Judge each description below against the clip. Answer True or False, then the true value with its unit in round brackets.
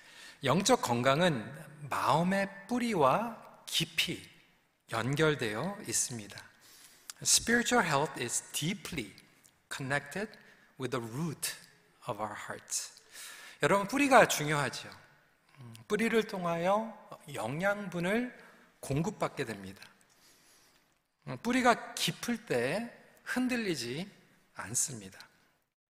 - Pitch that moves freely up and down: True (8.1 semitones)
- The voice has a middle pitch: True (180 Hz)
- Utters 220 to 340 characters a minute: True (270 characters per minute)